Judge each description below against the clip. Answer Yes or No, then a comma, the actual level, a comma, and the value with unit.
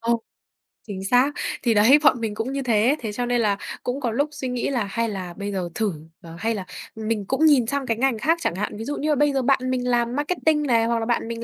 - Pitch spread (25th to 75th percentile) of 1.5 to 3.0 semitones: No, average, 3.9 semitones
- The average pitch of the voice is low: No, high, 235 Hz